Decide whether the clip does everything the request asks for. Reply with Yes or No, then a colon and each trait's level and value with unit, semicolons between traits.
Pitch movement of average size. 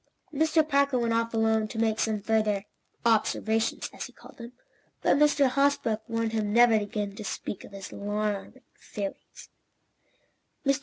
No: narrow, 2.3 semitones